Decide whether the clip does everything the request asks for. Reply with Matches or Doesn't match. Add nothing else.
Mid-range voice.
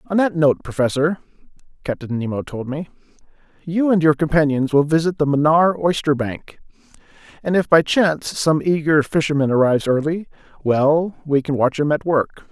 Matches